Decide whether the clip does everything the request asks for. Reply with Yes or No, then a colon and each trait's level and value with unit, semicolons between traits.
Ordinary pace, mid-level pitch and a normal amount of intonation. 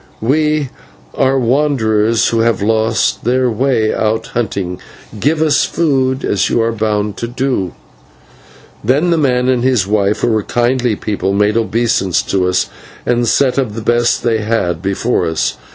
No: average, 160 wpm; low, 115 Hz; average, 3.6 semitones